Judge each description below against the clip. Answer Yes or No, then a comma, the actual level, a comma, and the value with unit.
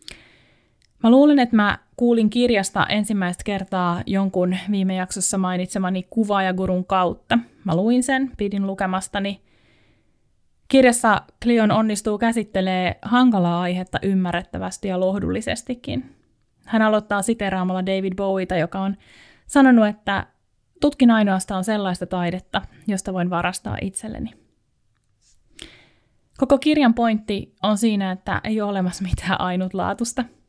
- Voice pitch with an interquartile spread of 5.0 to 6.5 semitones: No, average, 3.2 semitones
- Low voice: No, high, 200 Hz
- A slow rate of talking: No, average, 110 wpm